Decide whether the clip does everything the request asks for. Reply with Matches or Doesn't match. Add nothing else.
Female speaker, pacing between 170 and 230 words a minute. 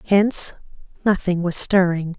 Doesn't match